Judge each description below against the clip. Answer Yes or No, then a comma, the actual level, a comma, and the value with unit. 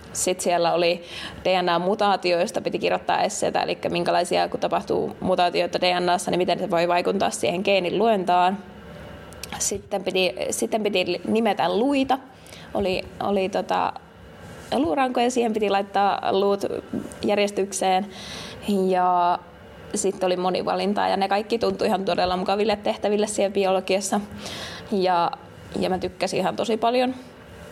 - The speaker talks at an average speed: Yes, average, 125 wpm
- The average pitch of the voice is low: No, high, 190 Hz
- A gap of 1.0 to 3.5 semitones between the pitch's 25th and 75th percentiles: Yes, narrow, 2.4 semitones